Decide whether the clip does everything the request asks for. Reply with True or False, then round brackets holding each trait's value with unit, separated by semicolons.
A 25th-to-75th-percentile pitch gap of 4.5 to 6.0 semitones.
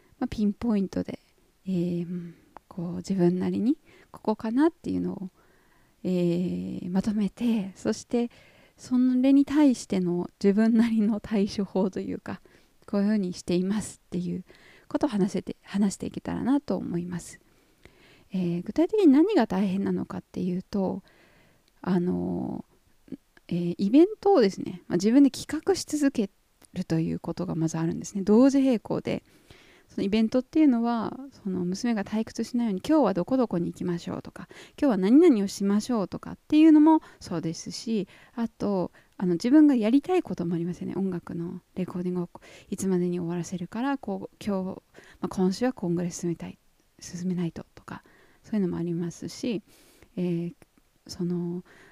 True (5.2 semitones)